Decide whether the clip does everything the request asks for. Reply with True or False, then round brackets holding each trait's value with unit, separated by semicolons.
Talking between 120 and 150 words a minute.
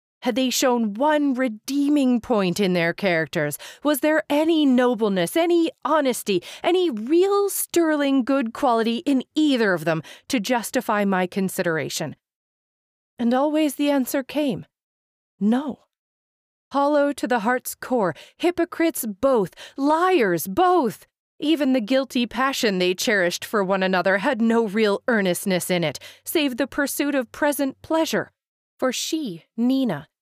True (135 wpm)